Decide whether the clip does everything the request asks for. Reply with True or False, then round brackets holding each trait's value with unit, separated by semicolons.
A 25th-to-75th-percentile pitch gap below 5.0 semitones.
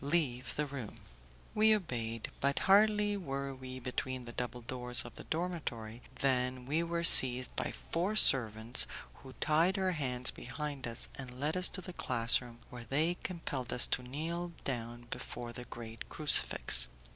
False (5.3 semitones)